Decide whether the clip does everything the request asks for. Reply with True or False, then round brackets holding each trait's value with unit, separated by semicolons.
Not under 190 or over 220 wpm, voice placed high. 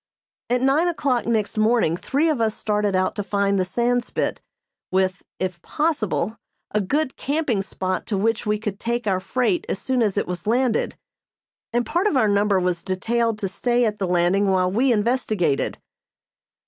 False (175 wpm; 215 Hz)